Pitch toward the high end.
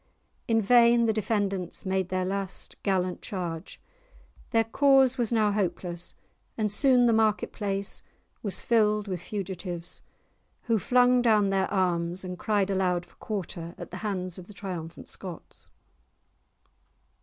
Yes: high, 200 Hz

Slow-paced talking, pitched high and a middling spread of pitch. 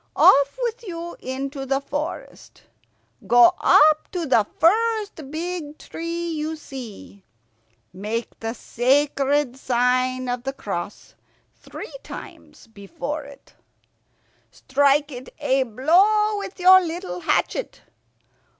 Yes: slow, 110 wpm; very high, 285 Hz; average, 4.9 semitones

